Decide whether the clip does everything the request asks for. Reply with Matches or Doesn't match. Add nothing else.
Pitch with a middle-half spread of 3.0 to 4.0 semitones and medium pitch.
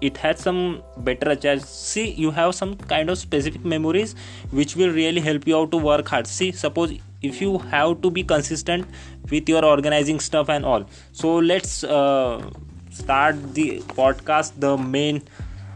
Matches